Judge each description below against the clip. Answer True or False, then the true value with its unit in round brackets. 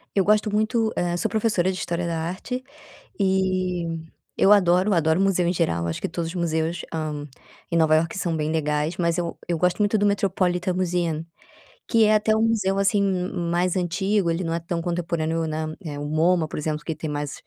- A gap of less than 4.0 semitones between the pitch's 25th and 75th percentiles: True (3.1 semitones)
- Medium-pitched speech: True (175 Hz)